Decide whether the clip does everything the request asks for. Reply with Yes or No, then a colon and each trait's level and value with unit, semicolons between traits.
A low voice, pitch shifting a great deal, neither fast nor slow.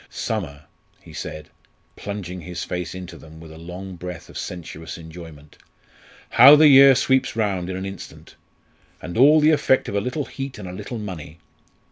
Yes: very low, 90 Hz; wide, 6.6 semitones; average, 175 wpm